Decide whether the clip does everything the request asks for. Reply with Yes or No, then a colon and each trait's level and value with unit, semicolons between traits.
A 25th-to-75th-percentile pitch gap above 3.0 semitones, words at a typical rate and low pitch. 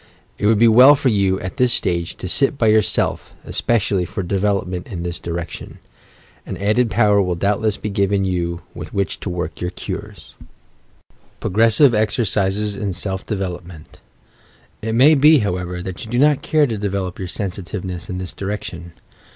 Yes: average, 3.5 semitones; average, 165 wpm; low, 100 Hz